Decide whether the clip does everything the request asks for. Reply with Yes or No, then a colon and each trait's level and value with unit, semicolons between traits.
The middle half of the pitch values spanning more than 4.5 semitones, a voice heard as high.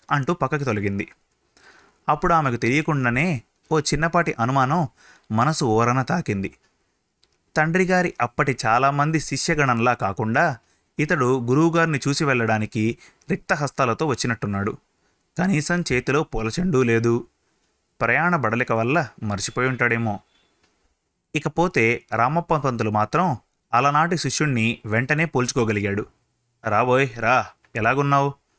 No: average, 5.2 semitones; low, 130 Hz